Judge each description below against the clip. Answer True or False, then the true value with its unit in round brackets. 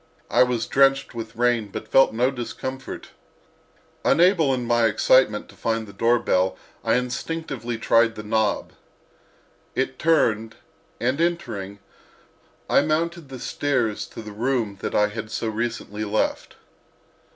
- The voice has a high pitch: False (120 Hz)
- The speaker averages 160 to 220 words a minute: False (135 wpm)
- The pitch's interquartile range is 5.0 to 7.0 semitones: False (3.5 semitones)